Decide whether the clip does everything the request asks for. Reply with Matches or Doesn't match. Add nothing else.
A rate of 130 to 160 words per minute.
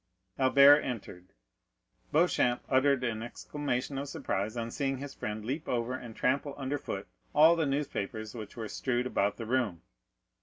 Matches